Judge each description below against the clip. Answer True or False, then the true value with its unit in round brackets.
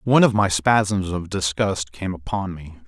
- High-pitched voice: False (95 Hz)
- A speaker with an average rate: True (190 wpm)